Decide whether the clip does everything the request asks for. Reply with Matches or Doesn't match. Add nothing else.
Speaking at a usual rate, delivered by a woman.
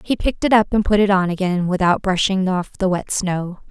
Doesn't match